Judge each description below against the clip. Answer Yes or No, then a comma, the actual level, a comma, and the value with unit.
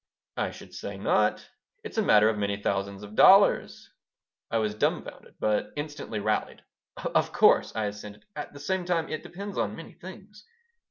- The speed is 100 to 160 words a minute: No, average, 170 wpm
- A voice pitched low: Yes, low, 115 Hz